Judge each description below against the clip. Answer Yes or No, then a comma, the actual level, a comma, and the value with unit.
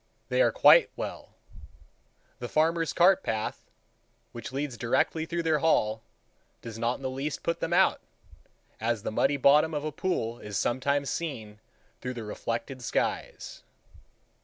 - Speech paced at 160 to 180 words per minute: No, average, 150 wpm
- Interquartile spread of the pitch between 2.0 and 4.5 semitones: No, wide, 5.6 semitones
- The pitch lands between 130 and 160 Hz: Yes, medium, 140 Hz